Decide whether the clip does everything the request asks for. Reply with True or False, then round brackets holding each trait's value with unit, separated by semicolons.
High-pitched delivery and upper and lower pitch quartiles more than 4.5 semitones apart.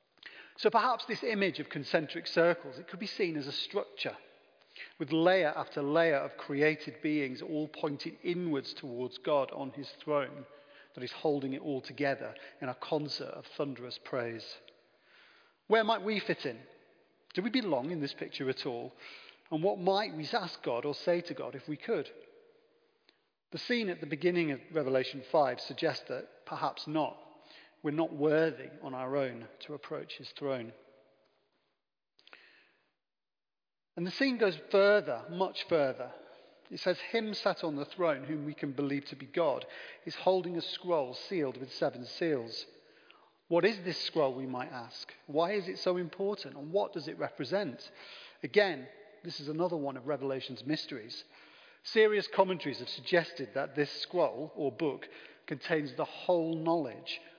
False (160 Hz; 5.2 semitones)